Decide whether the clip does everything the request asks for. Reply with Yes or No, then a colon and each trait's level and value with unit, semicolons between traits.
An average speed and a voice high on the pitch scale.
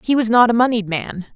No: fast, 265 wpm; high, 225 Hz